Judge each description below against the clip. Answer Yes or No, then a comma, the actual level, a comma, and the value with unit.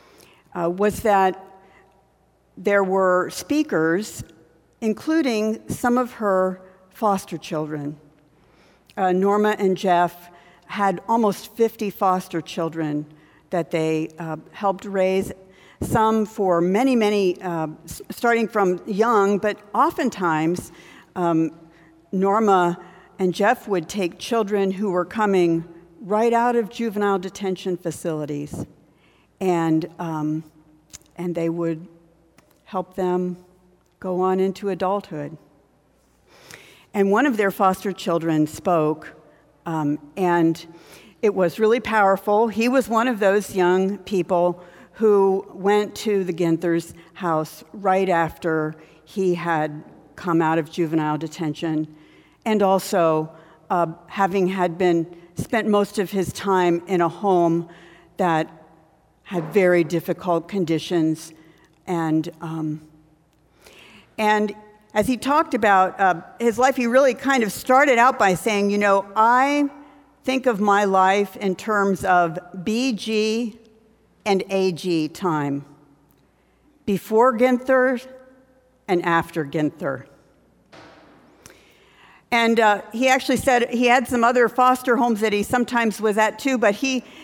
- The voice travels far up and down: No, average, 4.2 semitones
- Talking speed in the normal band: No, slow, 120 wpm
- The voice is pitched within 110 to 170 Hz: No, high, 190 Hz